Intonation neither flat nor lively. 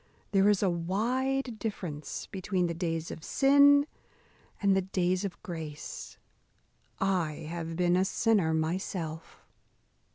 Yes: average, 3.9 semitones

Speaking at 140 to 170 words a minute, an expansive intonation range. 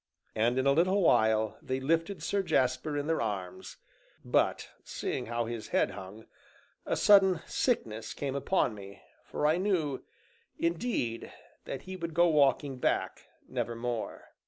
Yes: average, 145 wpm; wide, 6.5 semitones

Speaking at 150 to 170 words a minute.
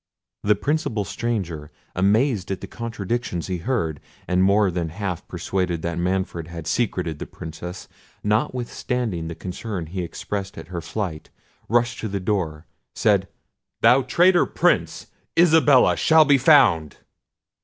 No: slow, 135 wpm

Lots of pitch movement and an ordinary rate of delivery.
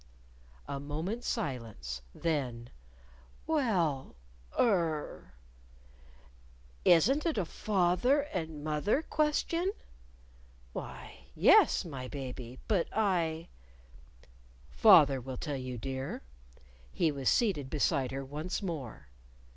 No: wide, 6.6 semitones; slow, 105 wpm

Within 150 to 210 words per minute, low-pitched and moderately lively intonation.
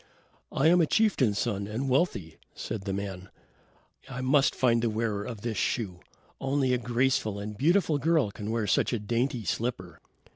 Yes: average, 175 wpm; low, 115 Hz; average, 4.6 semitones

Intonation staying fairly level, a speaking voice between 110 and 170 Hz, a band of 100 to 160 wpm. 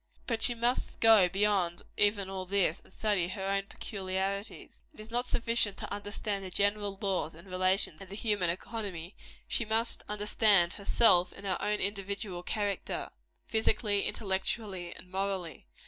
No: narrow, 2.2 semitones; high, 200 Hz; average, 155 wpm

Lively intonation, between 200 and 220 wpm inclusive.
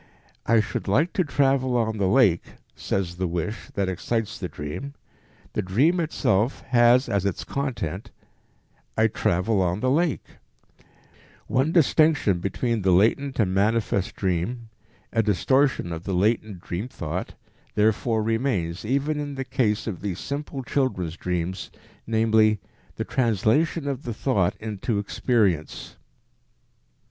No: wide, 5.7 semitones; slow, 135 wpm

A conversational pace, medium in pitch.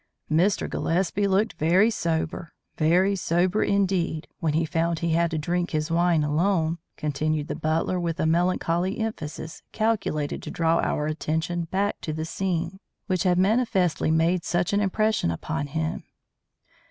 Yes: average, 155 wpm; medium, 170 Hz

